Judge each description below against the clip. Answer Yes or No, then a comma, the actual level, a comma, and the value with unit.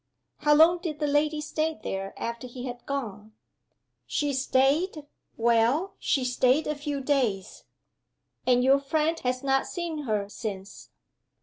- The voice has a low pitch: No, very high, 275 Hz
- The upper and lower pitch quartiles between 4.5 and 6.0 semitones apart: No, average, 3.9 semitones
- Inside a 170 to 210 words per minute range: No, average, 140 wpm